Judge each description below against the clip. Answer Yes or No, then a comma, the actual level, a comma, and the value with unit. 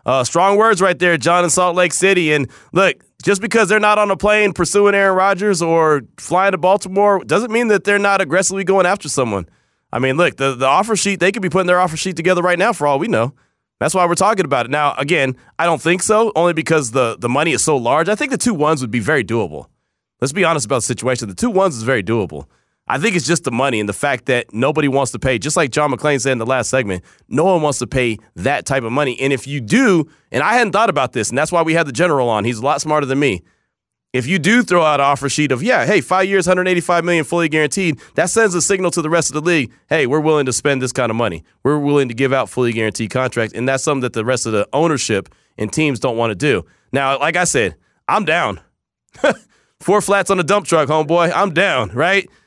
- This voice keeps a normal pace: No, fast, 260 wpm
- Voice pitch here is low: No, medium, 155 Hz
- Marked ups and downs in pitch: Yes, wide, 6.4 semitones